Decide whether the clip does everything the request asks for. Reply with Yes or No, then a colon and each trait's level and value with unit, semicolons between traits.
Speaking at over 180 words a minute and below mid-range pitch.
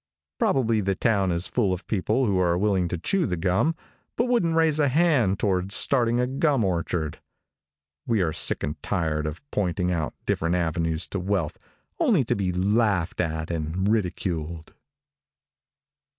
No: average, 160 wpm; very low, 95 Hz